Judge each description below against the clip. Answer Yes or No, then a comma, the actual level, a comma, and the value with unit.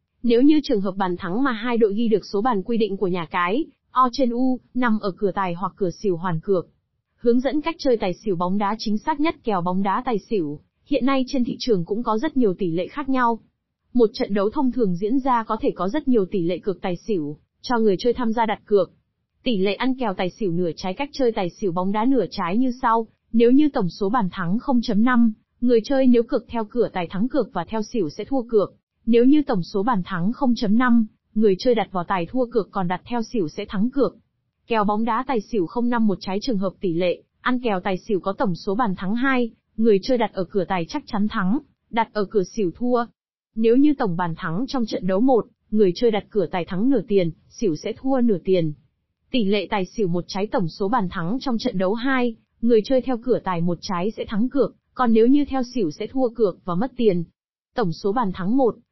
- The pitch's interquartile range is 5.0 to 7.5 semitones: No, average, 4.3 semitones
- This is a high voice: Yes, high, 220 Hz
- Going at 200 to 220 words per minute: No, average, 245 wpm